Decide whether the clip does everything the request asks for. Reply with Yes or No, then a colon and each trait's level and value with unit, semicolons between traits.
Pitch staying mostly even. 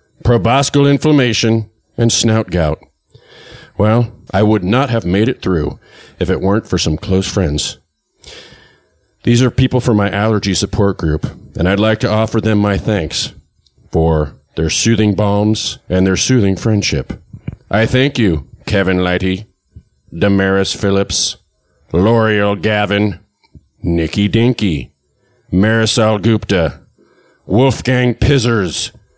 No: average, 3.6 semitones